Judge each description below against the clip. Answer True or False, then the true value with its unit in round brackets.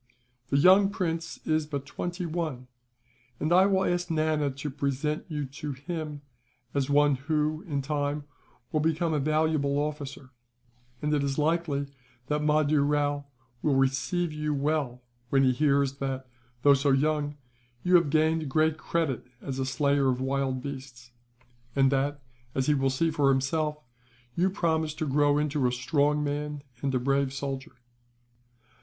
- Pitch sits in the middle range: True (145 Hz)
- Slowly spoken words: False (160 wpm)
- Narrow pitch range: True (2.2 semitones)